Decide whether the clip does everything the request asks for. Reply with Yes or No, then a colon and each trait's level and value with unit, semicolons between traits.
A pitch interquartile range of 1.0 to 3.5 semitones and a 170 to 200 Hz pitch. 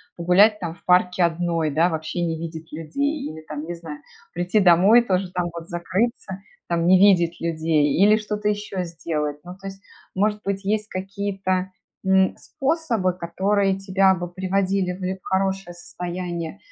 Yes: narrow, 2.5 semitones; medium, 185 Hz